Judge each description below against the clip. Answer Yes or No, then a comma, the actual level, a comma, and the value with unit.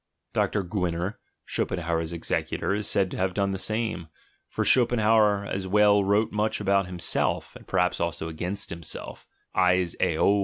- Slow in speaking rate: No, average, 160 wpm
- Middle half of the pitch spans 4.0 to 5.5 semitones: No, average, 2.9 semitones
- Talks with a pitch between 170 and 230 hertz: No, very low, 95 Hz